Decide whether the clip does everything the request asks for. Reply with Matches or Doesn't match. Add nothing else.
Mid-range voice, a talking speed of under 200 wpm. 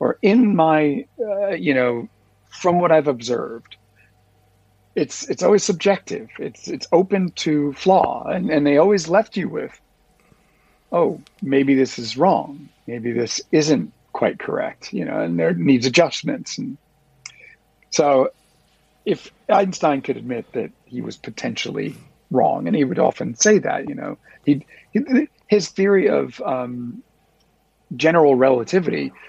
Matches